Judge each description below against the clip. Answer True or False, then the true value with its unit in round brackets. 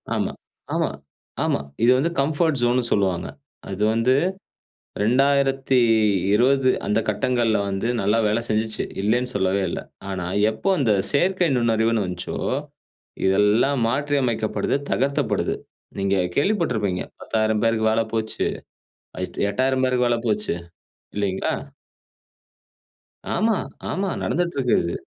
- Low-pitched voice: True (115 Hz)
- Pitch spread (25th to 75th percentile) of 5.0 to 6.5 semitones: False (4.4 semitones)